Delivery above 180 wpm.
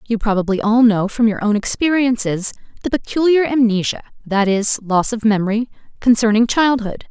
No: average, 150 wpm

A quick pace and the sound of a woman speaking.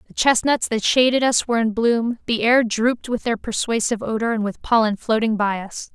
Yes: fast, 210 wpm; female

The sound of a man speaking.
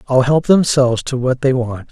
Yes: male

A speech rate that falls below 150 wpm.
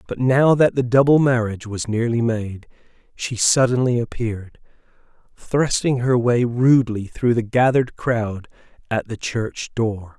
Yes: average, 140 wpm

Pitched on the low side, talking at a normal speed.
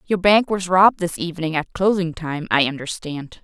No: medium, 175 Hz; average, 190 wpm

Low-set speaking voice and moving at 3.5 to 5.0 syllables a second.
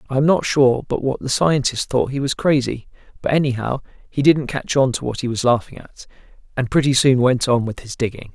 No: low, 130 Hz; 5.6 syllables/s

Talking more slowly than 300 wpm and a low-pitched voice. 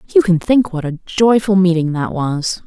No: average, 200 wpm; medium, 185 Hz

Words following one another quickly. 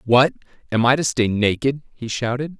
No: average, 185 wpm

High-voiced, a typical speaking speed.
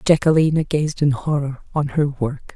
No: medium, 145 Hz; average, 165 wpm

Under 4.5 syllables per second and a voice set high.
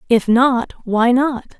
Yes: 3.4 syllables/s; high, 245 Hz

